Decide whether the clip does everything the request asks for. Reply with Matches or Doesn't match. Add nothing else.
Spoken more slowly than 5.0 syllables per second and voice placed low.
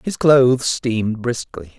Matches